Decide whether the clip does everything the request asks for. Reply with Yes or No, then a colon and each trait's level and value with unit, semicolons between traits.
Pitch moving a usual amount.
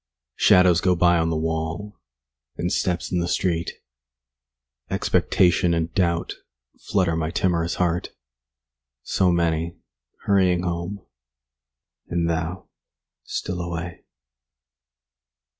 No: narrow, 1.4 semitones